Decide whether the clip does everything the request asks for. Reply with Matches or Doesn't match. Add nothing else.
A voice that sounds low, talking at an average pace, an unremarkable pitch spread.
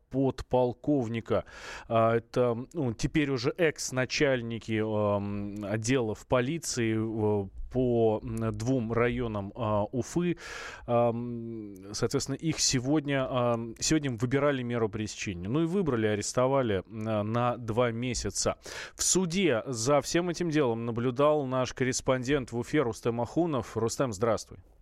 Doesn't match